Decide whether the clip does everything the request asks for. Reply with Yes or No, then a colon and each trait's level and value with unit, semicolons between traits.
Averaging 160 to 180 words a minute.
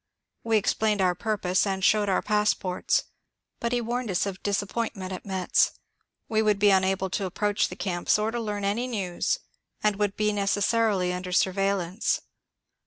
Yes: average, 170 wpm